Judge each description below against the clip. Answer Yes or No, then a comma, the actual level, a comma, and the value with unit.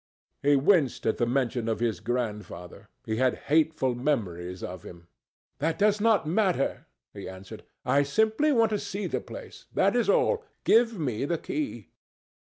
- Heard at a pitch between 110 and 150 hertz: Yes, medium, 140 Hz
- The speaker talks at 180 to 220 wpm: No, average, 160 wpm